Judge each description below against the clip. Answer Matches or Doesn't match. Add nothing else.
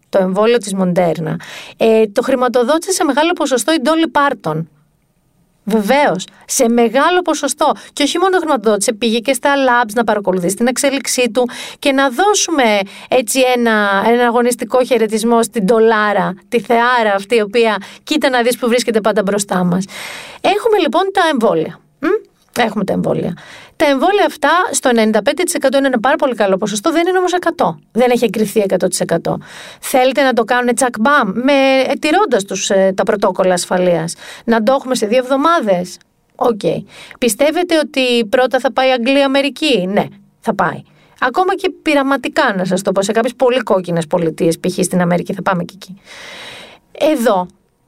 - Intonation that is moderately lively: Doesn't match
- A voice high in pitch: Matches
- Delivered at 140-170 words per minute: Matches